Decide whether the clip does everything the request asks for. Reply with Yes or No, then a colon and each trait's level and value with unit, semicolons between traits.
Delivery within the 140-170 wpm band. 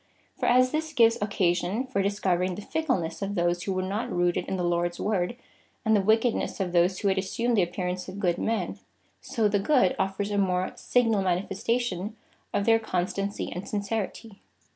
No: average, 185 wpm